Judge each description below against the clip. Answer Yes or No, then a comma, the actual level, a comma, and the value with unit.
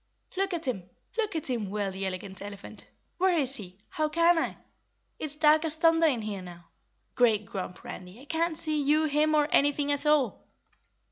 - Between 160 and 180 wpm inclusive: No, average, 190 wpm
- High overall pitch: Yes, very high, 285 Hz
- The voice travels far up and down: Yes, wide, 7.6 semitones